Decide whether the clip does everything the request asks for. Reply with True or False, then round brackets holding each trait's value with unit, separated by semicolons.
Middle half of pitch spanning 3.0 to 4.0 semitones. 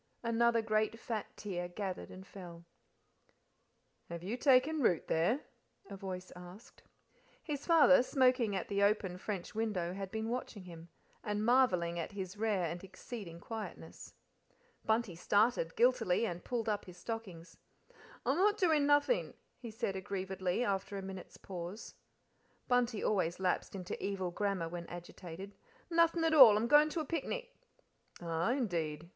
False (5.1 semitones)